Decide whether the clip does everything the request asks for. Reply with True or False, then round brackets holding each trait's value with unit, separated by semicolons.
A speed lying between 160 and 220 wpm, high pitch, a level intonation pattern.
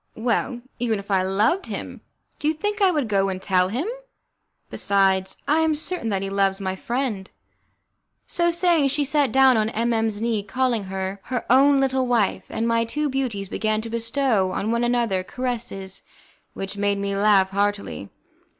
False (180 wpm; 225 Hz; 5.1 semitones)